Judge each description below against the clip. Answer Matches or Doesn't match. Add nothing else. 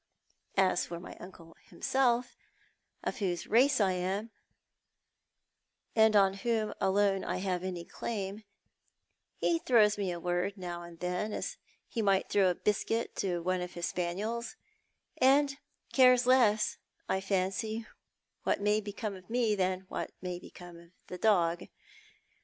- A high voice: Matches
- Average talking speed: Matches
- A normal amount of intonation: Matches